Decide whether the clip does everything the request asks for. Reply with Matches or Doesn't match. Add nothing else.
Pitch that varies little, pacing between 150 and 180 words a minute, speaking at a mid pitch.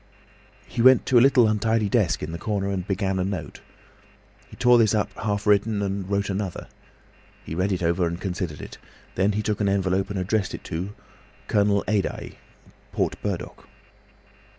Doesn't match